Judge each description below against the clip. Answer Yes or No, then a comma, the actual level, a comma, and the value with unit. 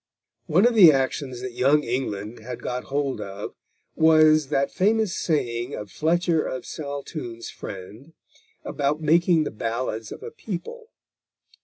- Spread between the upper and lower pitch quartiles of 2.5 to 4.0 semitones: No, average, 5.1 semitones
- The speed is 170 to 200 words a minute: No, average, 140 wpm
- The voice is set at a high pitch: No, medium, 140 Hz